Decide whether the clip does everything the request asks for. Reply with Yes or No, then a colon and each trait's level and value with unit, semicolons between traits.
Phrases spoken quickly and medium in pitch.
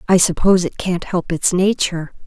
No: average, 185 wpm; medium, 180 Hz